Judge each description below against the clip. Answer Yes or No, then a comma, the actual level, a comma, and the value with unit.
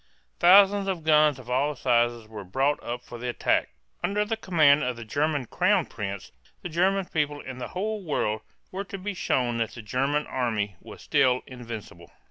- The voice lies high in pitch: No, low, 135 Hz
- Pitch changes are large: Yes, wide, 6.5 semitones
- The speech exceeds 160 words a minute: Yes, average, 185 wpm